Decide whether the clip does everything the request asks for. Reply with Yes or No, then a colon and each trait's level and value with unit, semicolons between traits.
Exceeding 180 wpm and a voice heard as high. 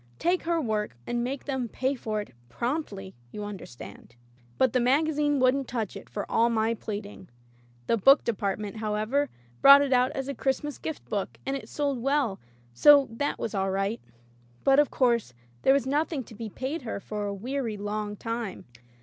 Yes: average, 190 wpm; high, 235 Hz